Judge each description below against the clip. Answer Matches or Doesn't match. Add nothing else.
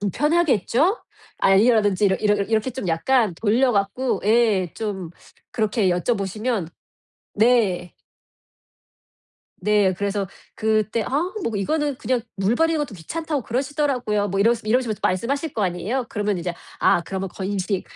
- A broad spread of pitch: Doesn't match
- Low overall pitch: Doesn't match